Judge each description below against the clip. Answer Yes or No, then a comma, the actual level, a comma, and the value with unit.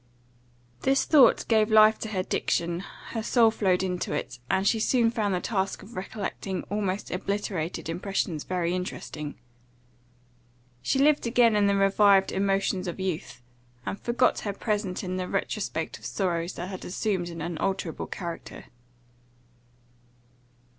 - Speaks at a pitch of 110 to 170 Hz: No, high, 195 Hz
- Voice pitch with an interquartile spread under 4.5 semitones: Yes, average, 3.0 semitones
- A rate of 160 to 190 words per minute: No, average, 140 wpm